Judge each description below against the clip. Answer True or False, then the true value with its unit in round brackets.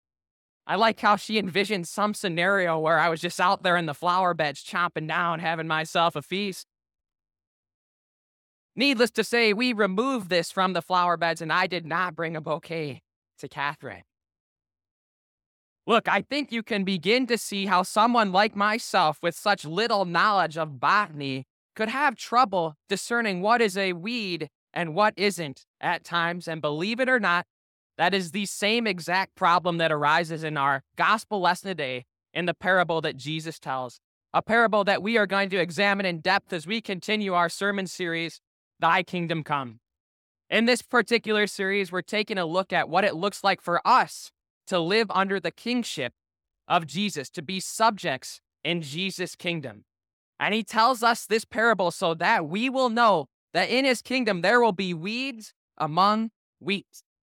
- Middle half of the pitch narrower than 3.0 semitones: False (4.6 semitones)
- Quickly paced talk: False (170 wpm)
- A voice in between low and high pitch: True (180 Hz)